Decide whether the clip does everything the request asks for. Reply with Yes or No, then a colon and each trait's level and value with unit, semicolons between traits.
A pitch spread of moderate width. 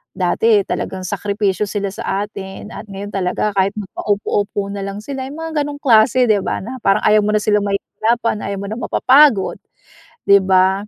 No: narrow, 2.2 semitones